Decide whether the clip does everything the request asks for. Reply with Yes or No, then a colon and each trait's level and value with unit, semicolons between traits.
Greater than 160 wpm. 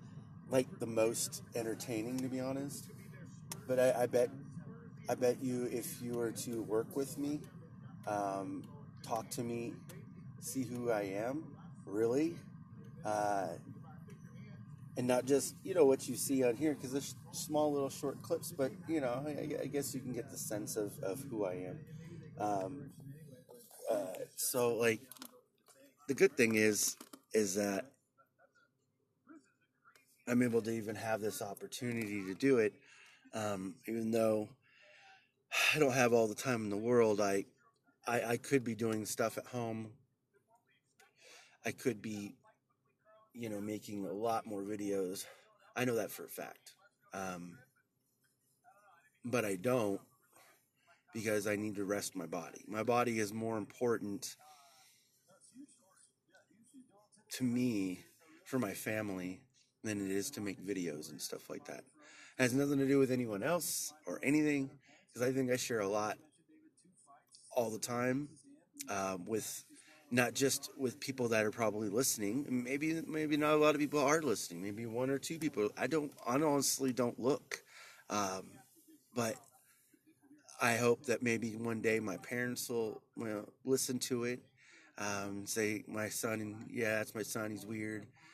No: average, 155 wpm